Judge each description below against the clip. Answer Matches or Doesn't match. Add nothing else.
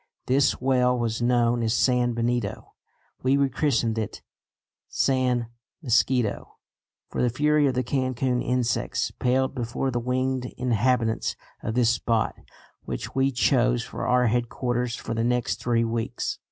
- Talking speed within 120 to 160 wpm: Matches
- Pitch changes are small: Matches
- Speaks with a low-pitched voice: Matches